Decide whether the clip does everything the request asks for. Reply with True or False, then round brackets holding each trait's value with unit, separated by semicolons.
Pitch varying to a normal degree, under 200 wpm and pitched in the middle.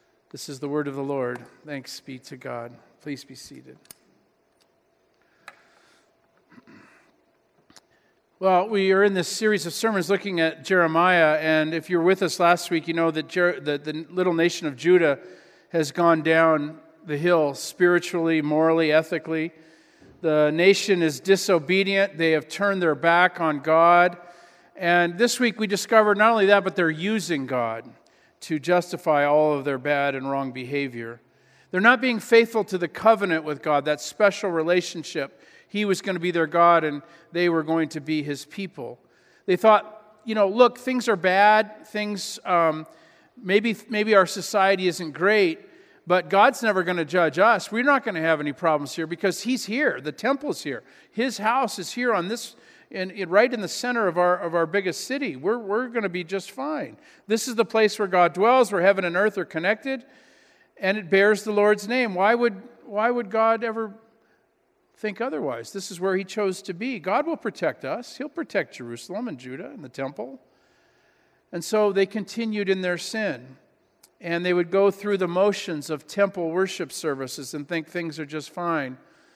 True (4.9 semitones; 180 wpm; 180 Hz)